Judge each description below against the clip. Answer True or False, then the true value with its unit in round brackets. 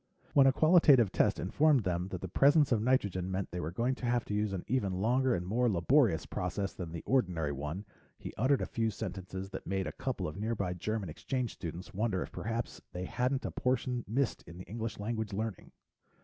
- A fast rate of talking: True (210 wpm)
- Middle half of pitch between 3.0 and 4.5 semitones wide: False (5.3 semitones)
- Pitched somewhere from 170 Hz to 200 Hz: False (105 Hz)